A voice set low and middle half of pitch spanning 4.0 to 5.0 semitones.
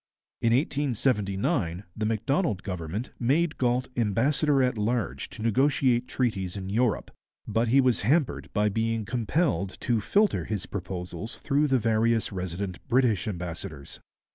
Yes: low, 115 Hz; average, 4.5 semitones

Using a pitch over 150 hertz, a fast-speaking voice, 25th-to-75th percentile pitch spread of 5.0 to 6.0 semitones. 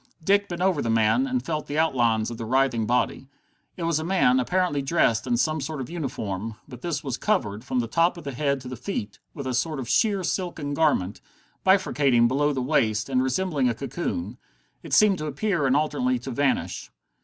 No: medium, 140 Hz; fast, 210 wpm; average, 5.3 semitones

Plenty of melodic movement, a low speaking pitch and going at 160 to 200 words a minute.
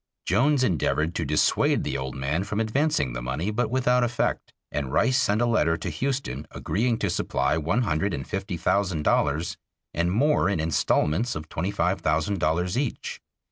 Yes: wide, 7.3 semitones; very low, 90 Hz; average, 180 wpm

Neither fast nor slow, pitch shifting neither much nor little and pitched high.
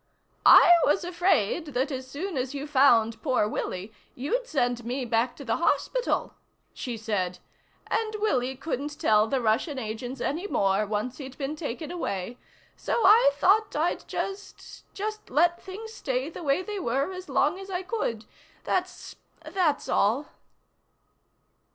No: average, 150 wpm; wide, 7.2 semitones; very high, 280 Hz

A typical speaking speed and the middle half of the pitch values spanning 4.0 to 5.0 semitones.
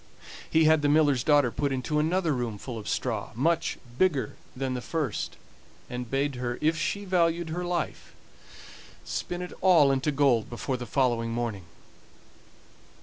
Yes: average, 155 wpm; average, 4.6 semitones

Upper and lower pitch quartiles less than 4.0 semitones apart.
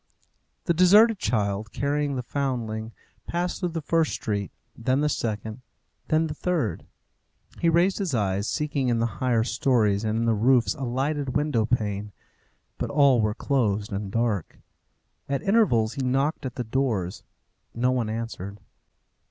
No: average, 5.0 semitones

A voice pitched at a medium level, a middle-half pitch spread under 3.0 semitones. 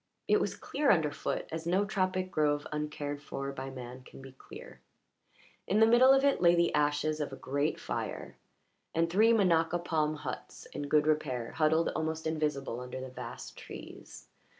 No: medium, 155 Hz; average, 3.5 semitones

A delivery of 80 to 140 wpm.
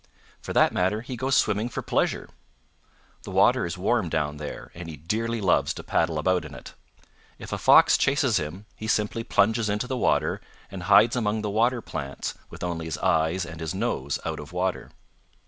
No: average, 195 wpm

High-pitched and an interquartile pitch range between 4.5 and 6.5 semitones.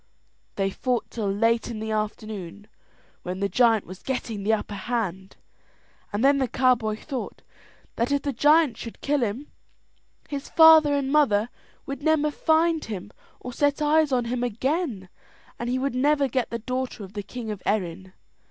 Yes: high, 240 Hz; average, 5.2 semitones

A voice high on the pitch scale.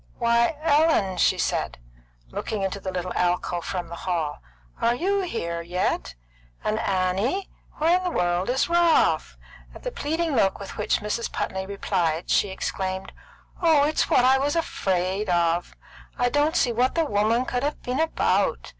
Yes: high, 215 Hz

